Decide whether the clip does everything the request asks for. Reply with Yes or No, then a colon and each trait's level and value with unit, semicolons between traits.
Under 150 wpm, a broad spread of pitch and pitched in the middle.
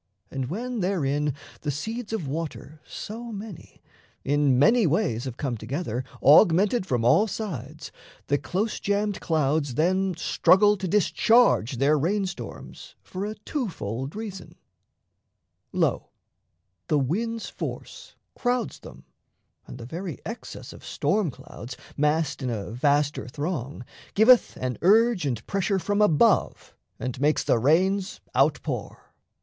Yes: slow, 135 wpm; wide, 6.9 semitones; medium, 165 Hz